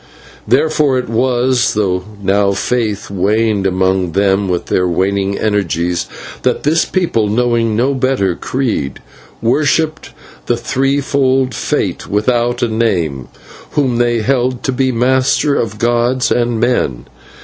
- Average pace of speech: No, slow, 125 wpm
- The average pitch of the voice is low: Yes, low, 115 Hz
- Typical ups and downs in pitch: Yes, average, 4.6 semitones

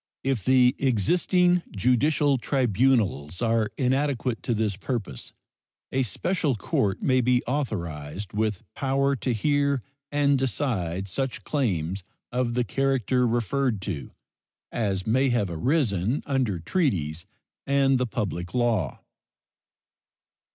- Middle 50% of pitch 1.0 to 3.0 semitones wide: No, average, 5.3 semitones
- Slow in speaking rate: Yes, slow, 115 wpm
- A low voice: Yes, low, 120 Hz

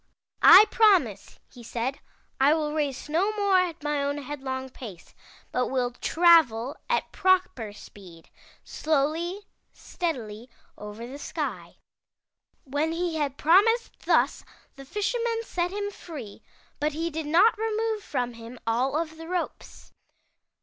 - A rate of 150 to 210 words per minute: No, slow, 135 wpm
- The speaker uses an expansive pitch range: Yes, wide, 6.2 semitones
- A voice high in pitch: Yes, very high, 300 Hz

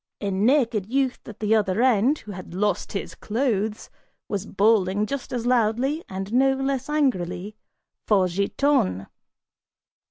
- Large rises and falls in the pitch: No, average, 4.9 semitones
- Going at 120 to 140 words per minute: Yes, slow, 135 wpm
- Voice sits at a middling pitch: No, high, 215 Hz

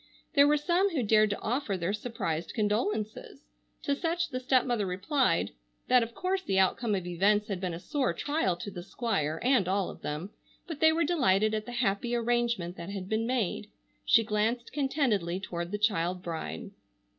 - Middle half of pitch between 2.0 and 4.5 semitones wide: No, wide, 5.4 semitones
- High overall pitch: Yes, high, 215 Hz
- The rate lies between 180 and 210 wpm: Yes, average, 185 wpm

